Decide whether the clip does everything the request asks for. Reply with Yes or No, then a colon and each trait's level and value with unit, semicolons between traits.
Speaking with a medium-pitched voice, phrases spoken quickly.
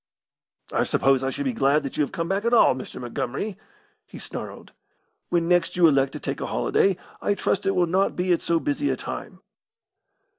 Yes: medium, 175 Hz; fast, 210 wpm